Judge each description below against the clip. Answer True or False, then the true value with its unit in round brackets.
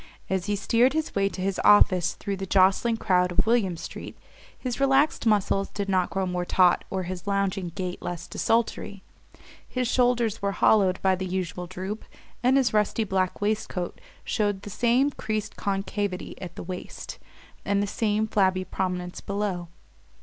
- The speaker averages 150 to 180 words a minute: True (165 wpm)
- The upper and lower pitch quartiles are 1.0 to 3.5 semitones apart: True (2.7 semitones)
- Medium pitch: False (195 Hz)